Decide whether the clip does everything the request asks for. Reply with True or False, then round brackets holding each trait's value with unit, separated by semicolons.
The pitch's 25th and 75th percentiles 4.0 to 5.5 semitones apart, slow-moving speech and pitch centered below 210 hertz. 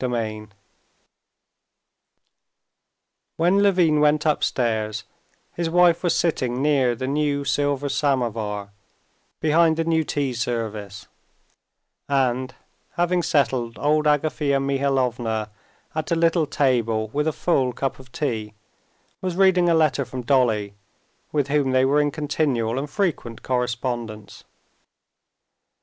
True (4.4 semitones; 120 wpm; 135 Hz)